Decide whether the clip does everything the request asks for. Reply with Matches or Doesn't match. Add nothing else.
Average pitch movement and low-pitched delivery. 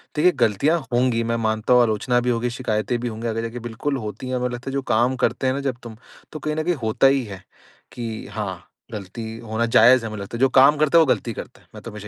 Matches